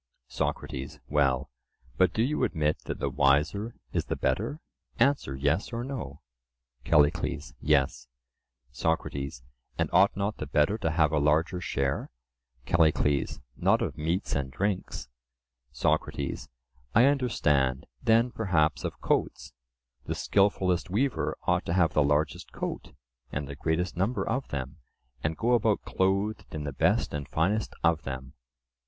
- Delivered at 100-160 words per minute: Yes, average, 140 wpm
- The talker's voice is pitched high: No, very low, 80 Hz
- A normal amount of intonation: No, wide, 6.5 semitones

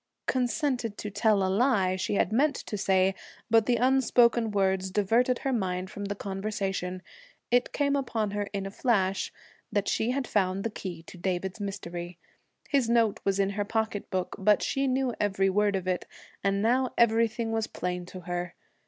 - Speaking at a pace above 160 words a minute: Yes, average, 180 wpm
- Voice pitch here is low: No, high, 205 Hz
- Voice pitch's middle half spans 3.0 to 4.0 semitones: Yes, average, 3.6 semitones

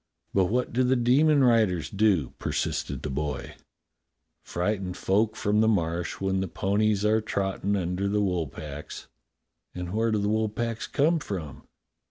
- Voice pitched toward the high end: No, low, 100 Hz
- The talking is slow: No, average, 165 wpm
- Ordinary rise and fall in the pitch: Yes, average, 3.5 semitones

